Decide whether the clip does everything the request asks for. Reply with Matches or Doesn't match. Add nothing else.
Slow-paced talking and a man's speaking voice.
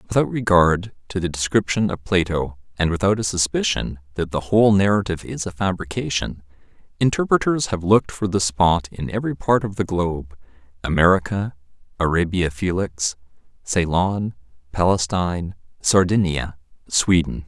Matches